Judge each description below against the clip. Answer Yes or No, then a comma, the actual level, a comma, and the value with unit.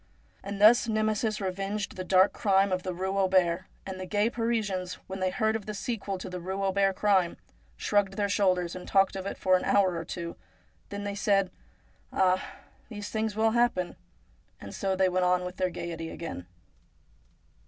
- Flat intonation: Yes, narrow, 2.0 semitones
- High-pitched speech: Yes, high, 195 Hz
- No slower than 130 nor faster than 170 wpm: No, average, 195 wpm